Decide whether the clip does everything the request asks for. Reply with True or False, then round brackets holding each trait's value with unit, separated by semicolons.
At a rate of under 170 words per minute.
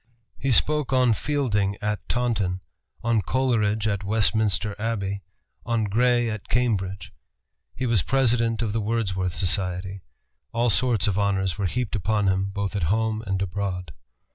True (145 wpm)